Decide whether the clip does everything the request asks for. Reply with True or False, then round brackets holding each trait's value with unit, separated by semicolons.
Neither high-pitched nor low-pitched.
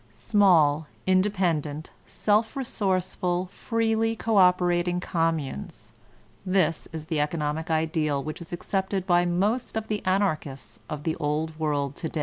True (175 Hz)